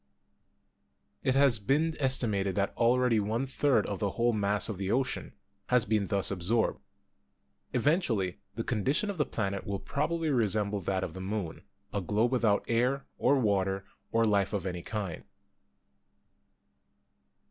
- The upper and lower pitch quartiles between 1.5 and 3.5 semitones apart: No, average, 4.2 semitones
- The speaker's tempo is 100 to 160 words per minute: Yes, average, 150 wpm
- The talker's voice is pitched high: No, low, 110 Hz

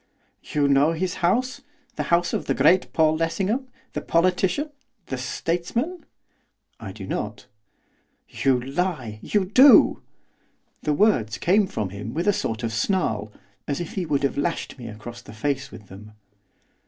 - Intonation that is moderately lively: No, wide, 8.0 semitones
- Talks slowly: No, average, 155 wpm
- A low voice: No, medium, 150 Hz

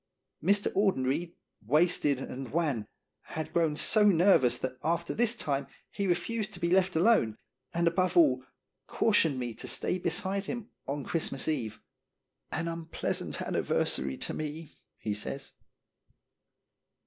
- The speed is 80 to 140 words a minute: Yes, slow, 135 wpm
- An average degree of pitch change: No, wide, 5.7 semitones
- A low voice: No, medium, 165 Hz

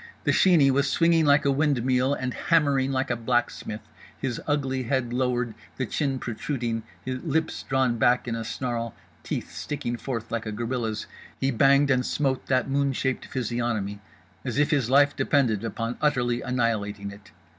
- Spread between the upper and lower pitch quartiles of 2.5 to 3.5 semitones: Yes, average, 2.9 semitones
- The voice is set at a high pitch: No, low, 130 Hz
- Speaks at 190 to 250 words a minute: No, average, 165 wpm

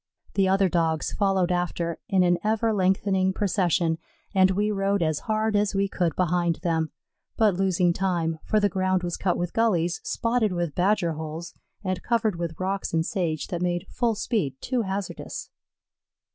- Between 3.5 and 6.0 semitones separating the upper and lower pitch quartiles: No, average, 2.8 semitones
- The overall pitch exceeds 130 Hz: Yes, medium, 185 Hz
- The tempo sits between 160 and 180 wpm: Yes, average, 170 wpm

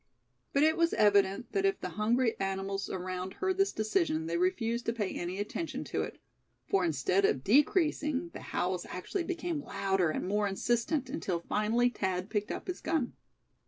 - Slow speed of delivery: No, average, 175 wpm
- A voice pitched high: Yes, high, 210 Hz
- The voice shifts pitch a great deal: Yes, wide, 7.6 semitones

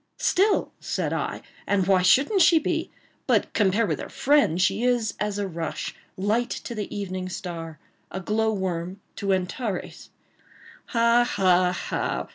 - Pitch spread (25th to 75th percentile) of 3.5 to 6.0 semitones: Yes, average, 4.3 semitones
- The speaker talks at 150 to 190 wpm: No, average, 140 wpm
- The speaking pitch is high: Yes, high, 200 Hz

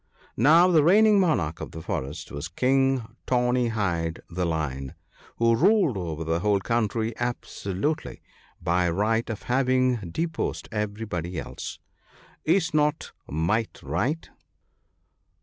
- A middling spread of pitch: No, wide, 7.7 semitones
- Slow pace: Yes, slow, 120 wpm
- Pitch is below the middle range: Yes, low, 110 Hz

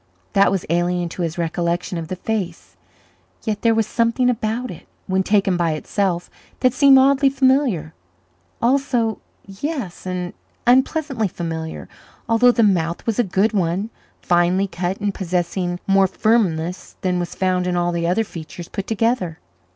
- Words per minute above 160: No, average, 155 wpm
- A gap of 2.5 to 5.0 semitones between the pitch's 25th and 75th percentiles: Yes, average, 4.6 semitones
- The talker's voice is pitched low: No, high, 190 Hz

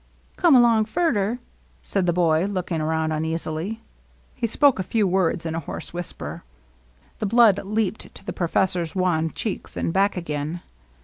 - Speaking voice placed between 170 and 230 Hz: Yes, medium, 185 Hz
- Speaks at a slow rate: No, average, 160 wpm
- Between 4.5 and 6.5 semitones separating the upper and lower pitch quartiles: Yes, average, 4.8 semitones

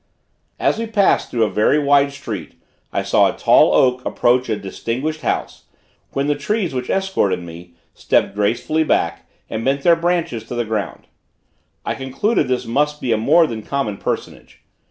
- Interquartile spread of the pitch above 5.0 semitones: Yes, wide, 5.6 semitones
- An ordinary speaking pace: Yes, average, 175 wpm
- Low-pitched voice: Yes, low, 130 Hz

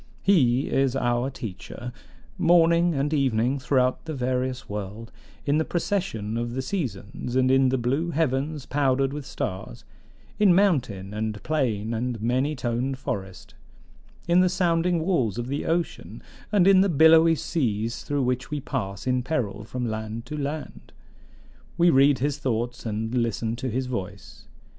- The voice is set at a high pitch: No, low, 130 Hz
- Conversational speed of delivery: Yes, average, 155 wpm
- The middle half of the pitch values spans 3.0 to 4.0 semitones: No, average, 4.8 semitones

